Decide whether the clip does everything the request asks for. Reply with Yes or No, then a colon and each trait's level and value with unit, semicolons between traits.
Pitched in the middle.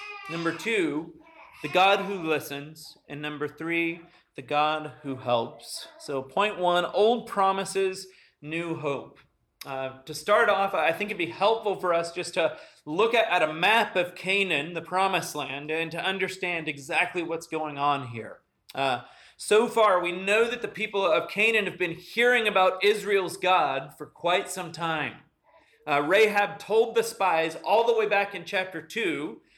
Yes: medium, 180 Hz